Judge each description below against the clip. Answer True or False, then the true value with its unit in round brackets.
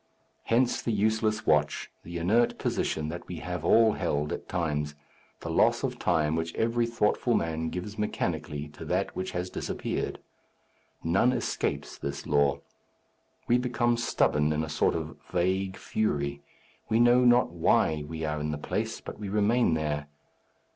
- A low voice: True (90 Hz)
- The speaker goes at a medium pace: True (160 wpm)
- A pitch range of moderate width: False (6.6 semitones)